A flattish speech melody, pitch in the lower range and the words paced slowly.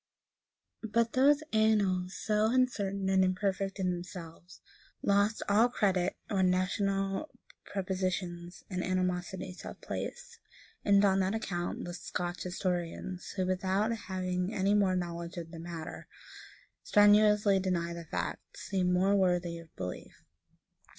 No: narrow, 2.2 semitones; medium, 185 Hz; slow, 130 wpm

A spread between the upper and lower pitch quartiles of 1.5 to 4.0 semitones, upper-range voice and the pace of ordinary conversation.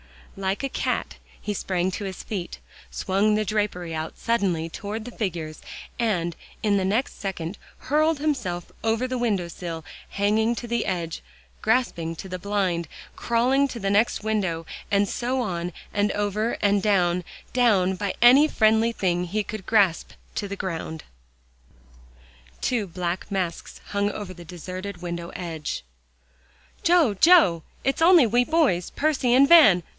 No: average, 4.7 semitones; high, 200 Hz; average, 150 wpm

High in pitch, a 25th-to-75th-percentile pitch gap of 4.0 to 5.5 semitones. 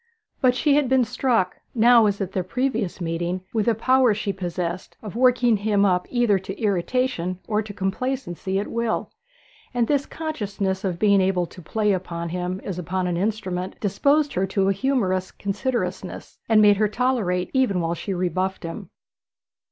Yes: high, 200 Hz; average, 4.6 semitones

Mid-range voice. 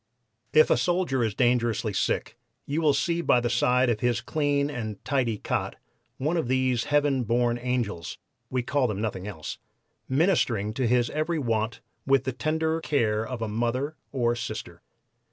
No: low, 125 Hz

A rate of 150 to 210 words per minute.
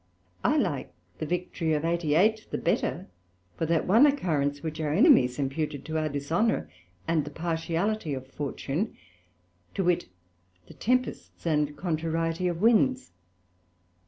No: slow, 135 wpm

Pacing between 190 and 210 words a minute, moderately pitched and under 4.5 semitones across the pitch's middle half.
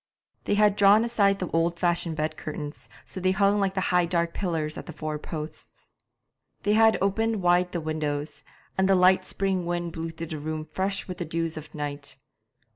Yes: average, 200 wpm; medium, 175 Hz; average, 3.6 semitones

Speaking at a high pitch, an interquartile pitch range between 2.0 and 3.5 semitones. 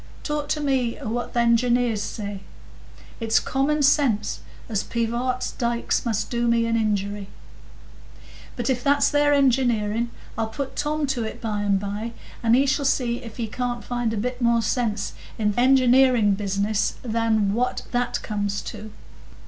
Yes: high, 235 Hz; average, 2.8 semitones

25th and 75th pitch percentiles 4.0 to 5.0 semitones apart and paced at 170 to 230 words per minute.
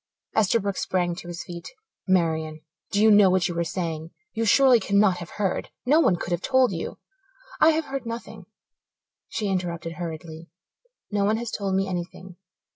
Yes: average, 4.3 semitones; average, 180 wpm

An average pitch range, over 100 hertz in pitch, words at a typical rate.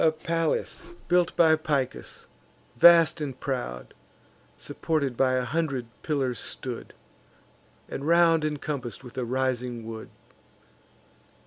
No: average, 4.2 semitones; medium, 140 Hz; slow, 110 wpm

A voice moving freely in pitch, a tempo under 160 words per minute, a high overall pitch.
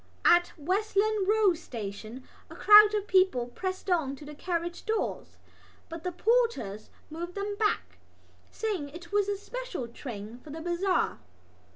Yes: wide, 6.1 semitones; average, 150 wpm; very high, 355 Hz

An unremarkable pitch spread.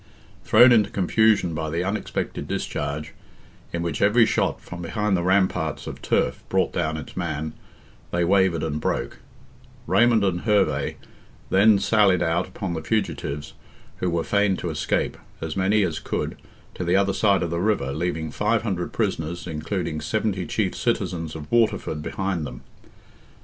Yes: average, 4.1 semitones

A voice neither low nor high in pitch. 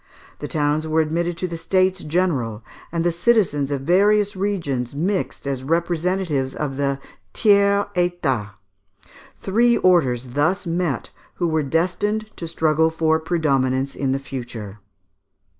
Yes: medium, 160 Hz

